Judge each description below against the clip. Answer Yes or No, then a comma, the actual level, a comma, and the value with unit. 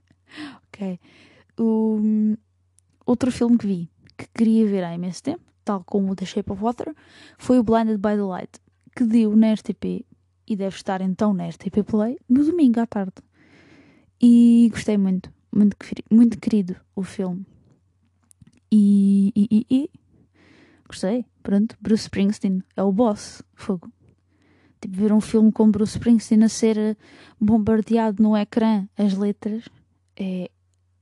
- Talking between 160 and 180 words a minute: No, average, 140 wpm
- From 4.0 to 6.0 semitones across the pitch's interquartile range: No, average, 2.9 semitones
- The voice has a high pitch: Yes, high, 210 Hz